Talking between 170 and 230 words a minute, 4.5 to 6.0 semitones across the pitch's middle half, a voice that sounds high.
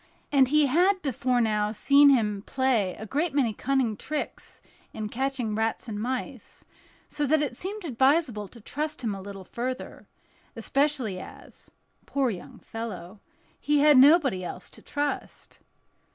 No: average, 140 wpm; average, 5.2 semitones; very high, 255 Hz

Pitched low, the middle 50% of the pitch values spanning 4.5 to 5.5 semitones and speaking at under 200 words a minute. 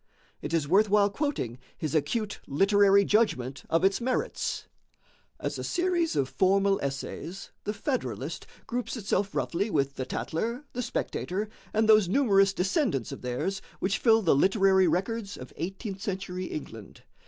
No: high, 195 Hz; average, 4.8 semitones; average, 150 wpm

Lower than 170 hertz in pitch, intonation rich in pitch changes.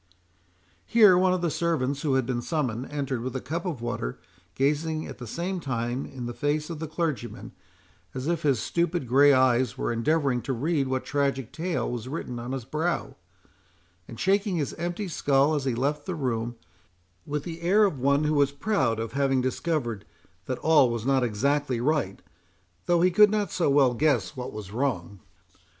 No: medium, 140 Hz; average, 4.6 semitones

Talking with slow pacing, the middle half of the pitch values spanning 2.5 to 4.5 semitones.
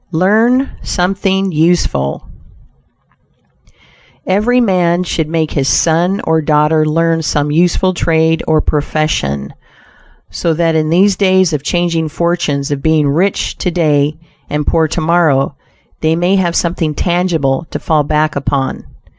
Yes: slow, 130 wpm; average, 2.8 semitones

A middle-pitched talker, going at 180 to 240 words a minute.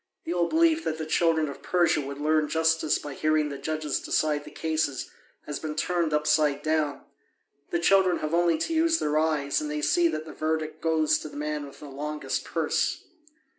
Yes: medium, 155 Hz; average, 200 wpm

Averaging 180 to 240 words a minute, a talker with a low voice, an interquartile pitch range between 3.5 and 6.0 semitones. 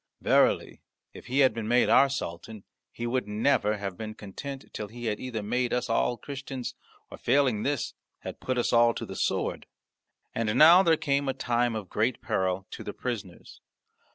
Yes: average, 185 wpm; low, 120 Hz; average, 3.8 semitones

